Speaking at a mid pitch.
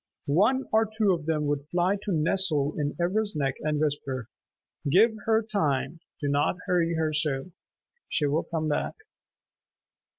Yes: medium, 160 Hz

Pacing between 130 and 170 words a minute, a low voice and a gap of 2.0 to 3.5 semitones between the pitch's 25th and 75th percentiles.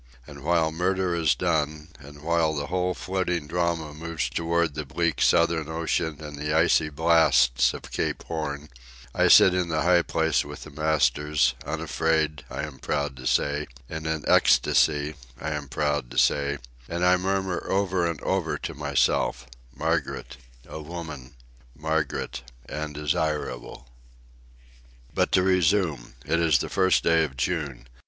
Yes: average, 150 wpm; very low, 80 Hz; narrow, 2.6 semitones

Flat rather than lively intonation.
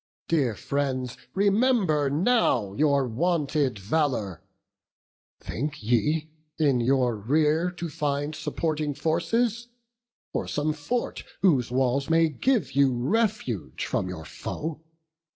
No: average, 4.4 semitones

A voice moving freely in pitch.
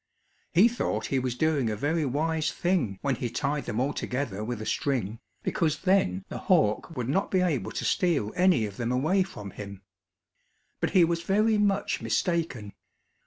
Yes: wide, 7.1 semitones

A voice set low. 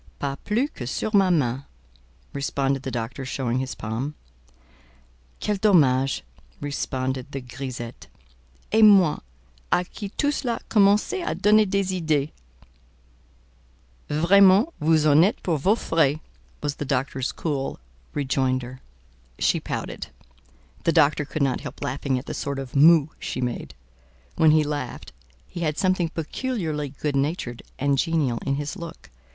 No: medium, 145 Hz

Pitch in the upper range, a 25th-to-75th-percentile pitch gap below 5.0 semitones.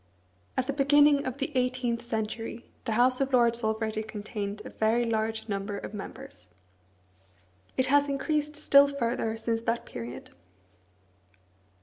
Yes: high, 235 Hz; average, 3.8 semitones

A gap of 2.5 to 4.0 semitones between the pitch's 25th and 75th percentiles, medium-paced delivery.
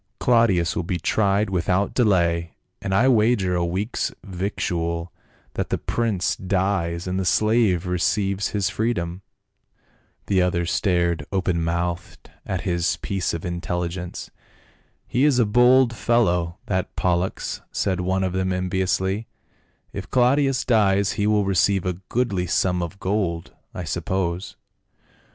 Yes: average, 3.0 semitones; average, 145 wpm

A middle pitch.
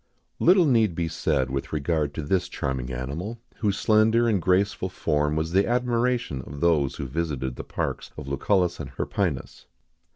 No: very low, 85 Hz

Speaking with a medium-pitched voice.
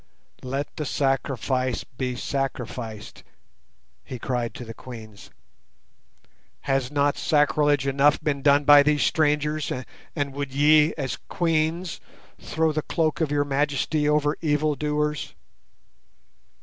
Yes: medium, 145 Hz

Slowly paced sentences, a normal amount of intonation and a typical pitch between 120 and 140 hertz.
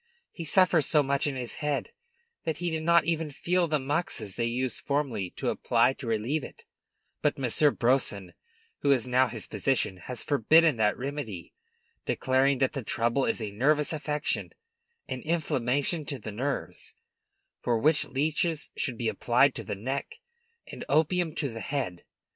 No: average, 165 wpm; average, 4.3 semitones; low, 135 Hz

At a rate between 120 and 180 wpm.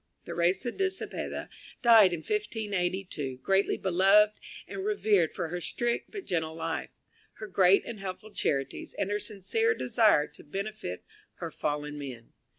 Yes: average, 145 wpm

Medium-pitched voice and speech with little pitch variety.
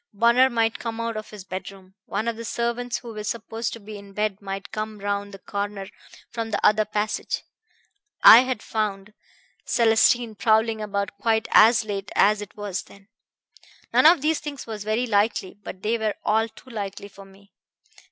No: high, 215 Hz; narrow, 2.3 semitones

